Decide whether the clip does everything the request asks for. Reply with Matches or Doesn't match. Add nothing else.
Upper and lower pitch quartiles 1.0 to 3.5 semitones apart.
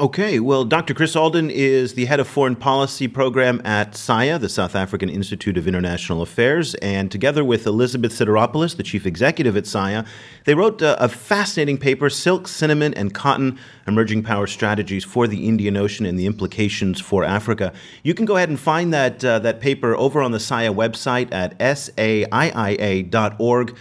Doesn't match